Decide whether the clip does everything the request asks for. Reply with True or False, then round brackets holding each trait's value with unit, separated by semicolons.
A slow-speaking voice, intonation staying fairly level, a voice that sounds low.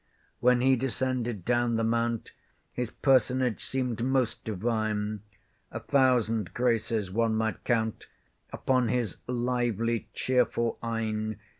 True (115 wpm; 2.1 semitones; 115 Hz)